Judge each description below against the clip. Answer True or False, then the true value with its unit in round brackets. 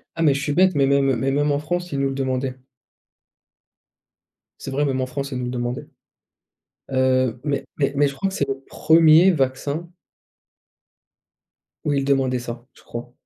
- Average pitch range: False (2.1 semitones)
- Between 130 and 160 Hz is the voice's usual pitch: True (135 Hz)